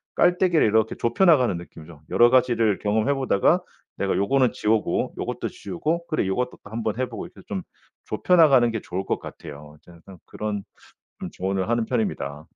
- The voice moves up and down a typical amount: No, wide, 5.7 semitones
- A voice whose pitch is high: No, low, 110 Hz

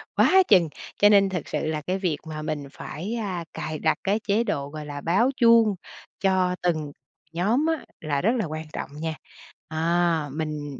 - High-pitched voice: No, medium, 170 Hz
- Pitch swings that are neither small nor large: Yes, average, 4.7 semitones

